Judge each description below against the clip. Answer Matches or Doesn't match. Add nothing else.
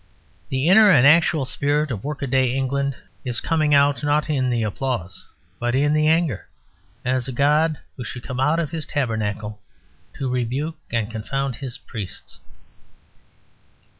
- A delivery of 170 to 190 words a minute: Doesn't match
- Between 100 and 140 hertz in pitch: Matches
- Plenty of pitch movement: Doesn't match